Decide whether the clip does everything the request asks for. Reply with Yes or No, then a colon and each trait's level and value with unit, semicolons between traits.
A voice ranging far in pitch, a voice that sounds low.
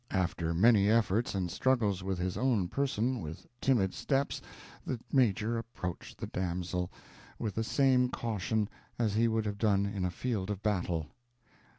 No: average, 4.2 semitones; low, 105 Hz